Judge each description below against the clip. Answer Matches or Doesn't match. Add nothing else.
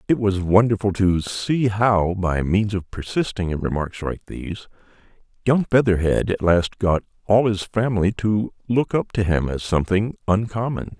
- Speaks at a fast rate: Doesn't match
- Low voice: Matches